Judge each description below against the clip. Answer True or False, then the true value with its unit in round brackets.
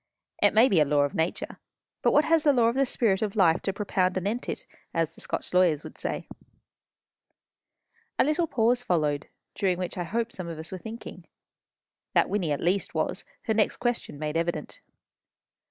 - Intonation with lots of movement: True (5.7 semitones)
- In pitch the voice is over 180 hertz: True (190 Hz)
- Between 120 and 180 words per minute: False (190 wpm)